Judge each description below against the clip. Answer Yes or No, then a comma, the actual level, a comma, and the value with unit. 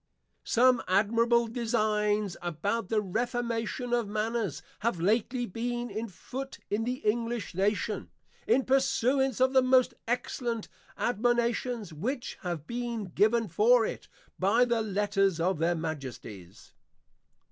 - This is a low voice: No, high, 225 Hz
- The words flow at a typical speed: No, slow, 125 wpm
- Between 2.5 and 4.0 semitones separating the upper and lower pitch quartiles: Yes, average, 3.3 semitones